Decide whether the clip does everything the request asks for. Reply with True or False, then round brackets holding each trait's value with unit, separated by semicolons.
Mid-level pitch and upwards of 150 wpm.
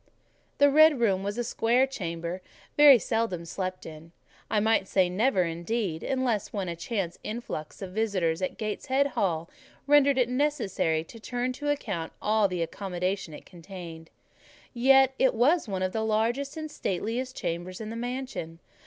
False (215 Hz; 160 wpm)